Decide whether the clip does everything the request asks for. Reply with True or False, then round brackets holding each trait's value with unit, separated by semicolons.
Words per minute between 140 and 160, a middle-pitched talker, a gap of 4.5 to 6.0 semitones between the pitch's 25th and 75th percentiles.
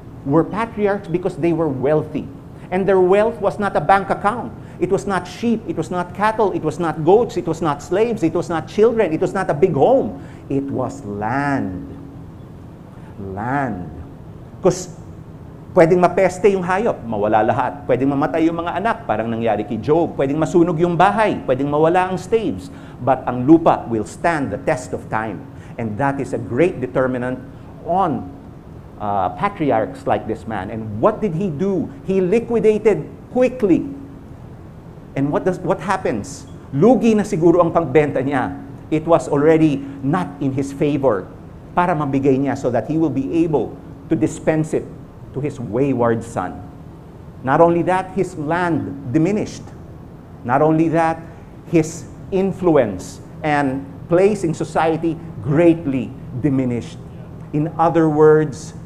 True (155 wpm; 160 Hz; 4.8 semitones)